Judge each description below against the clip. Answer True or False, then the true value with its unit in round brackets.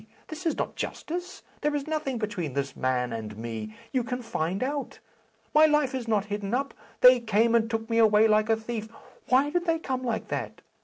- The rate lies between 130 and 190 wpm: False (205 wpm)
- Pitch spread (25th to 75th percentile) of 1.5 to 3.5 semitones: False (5.1 semitones)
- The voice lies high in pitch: True (230 Hz)